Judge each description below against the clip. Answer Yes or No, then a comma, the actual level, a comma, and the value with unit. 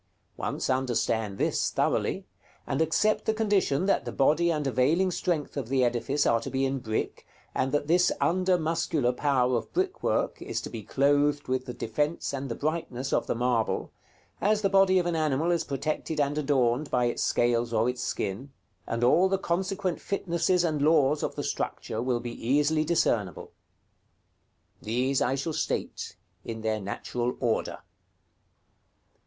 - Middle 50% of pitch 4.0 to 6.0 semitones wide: Yes, average, 5.3 semitones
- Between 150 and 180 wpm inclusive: Yes, average, 165 wpm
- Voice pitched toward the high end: No, medium, 140 Hz